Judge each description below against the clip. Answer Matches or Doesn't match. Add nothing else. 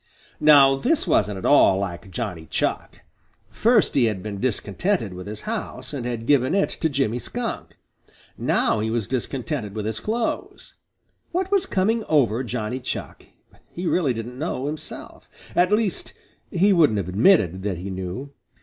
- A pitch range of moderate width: Doesn't match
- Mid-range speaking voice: Doesn't match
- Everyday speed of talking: Matches